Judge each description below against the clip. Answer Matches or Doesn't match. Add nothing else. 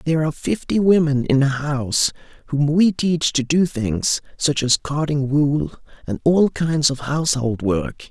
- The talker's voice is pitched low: Doesn't match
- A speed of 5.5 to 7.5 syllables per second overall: Doesn't match